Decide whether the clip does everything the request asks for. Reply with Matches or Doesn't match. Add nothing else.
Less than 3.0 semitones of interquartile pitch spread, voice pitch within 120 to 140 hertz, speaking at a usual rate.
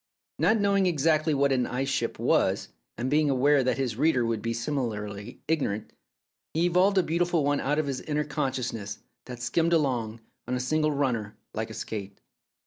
Doesn't match